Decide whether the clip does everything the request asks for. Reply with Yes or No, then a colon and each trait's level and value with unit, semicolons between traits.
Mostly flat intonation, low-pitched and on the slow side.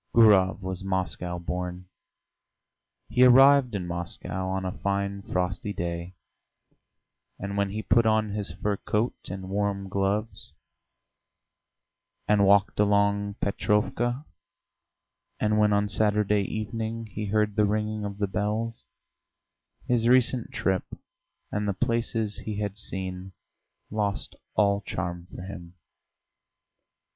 Yes: narrow, 2.1 semitones; low, 100 Hz; slow, 120 wpm